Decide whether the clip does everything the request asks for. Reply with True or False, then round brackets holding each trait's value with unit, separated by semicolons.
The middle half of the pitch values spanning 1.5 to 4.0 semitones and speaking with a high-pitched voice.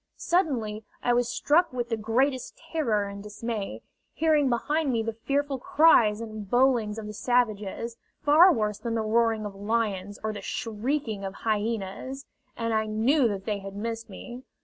True (3.6 semitones; 230 Hz)